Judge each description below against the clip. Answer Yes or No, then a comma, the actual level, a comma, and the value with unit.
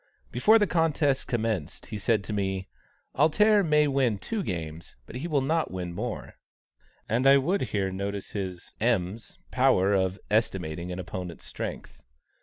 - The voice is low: Yes, low, 105 Hz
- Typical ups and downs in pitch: No, wide, 6.8 semitones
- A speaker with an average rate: Yes, average, 155 wpm